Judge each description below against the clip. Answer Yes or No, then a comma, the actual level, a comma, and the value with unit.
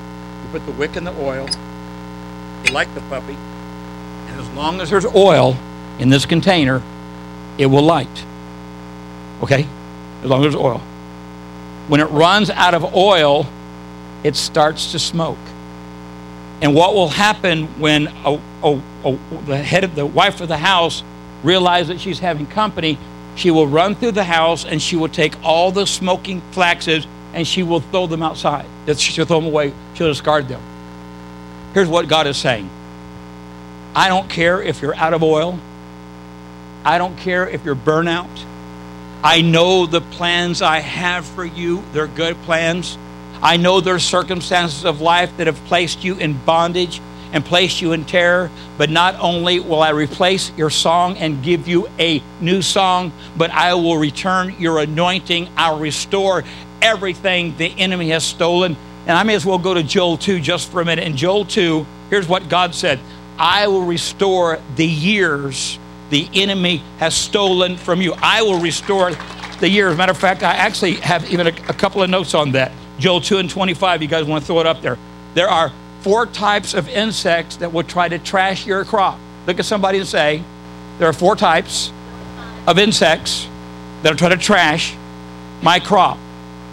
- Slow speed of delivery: No, average, 175 wpm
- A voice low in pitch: No, medium, 160 Hz